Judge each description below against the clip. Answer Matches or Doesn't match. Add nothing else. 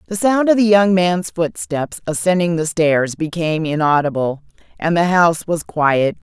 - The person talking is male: Doesn't match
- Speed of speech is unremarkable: Matches